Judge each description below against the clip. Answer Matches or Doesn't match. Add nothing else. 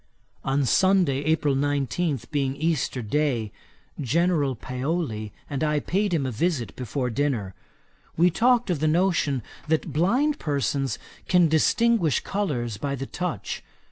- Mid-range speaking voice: Matches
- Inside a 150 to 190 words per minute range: Doesn't match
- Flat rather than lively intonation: Doesn't match